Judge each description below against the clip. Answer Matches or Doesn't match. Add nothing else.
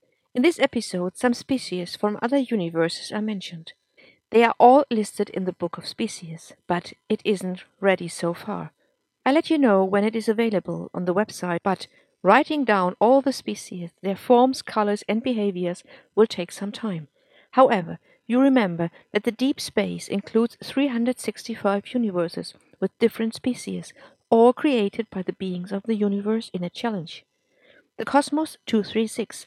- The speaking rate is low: Doesn't match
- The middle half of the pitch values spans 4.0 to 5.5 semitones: Matches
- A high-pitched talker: Matches